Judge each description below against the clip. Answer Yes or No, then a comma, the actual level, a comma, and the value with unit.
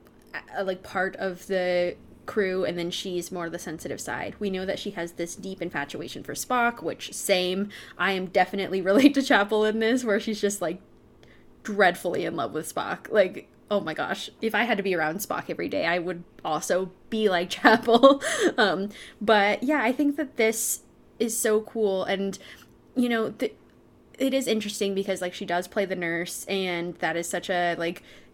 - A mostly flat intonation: No, average, 3.5 semitones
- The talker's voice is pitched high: Yes, high, 195 Hz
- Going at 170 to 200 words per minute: Yes, average, 190 wpm